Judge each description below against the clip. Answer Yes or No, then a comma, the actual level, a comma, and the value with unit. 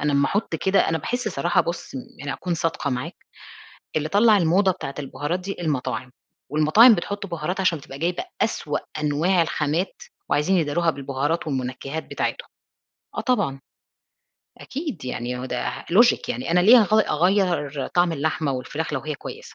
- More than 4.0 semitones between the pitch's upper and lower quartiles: Yes, average, 4.7 semitones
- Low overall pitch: No, medium, 160 Hz